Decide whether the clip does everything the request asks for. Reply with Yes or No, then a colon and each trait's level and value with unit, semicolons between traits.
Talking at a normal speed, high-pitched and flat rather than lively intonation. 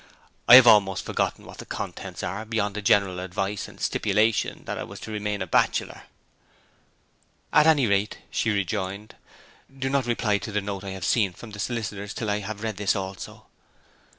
No: average, 185 wpm; low, 105 Hz; narrow, 2.2 semitones